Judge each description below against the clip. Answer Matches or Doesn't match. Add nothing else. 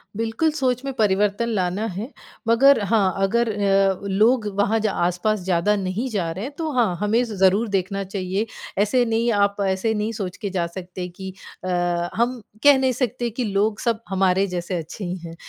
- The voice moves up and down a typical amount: Matches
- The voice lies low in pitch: Doesn't match